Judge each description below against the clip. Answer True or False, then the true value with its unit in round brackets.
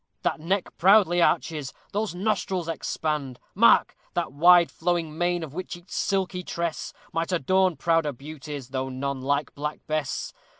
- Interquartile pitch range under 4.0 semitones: True (3.5 semitones)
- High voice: False (165 Hz)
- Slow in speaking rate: False (145 wpm)